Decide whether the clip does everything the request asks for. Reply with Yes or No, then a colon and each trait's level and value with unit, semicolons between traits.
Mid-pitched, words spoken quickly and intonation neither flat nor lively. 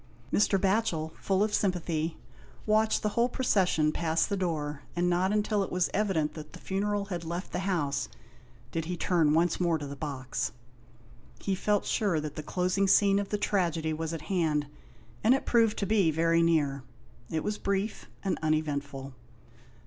No: medium, 175 Hz; average, 175 wpm; average, 4.2 semitones